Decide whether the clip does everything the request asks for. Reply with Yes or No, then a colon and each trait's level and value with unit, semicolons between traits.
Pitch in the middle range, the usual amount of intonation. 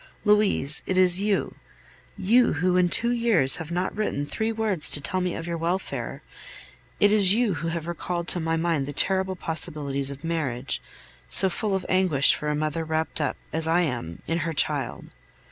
Yes: medium, 170 Hz; average, 3.7 semitones